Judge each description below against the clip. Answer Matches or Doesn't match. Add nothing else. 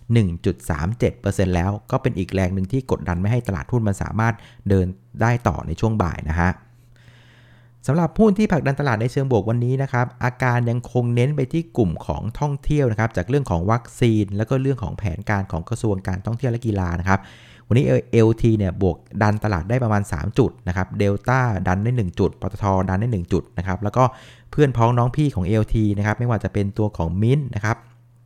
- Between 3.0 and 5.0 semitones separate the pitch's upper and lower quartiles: Matches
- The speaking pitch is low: Matches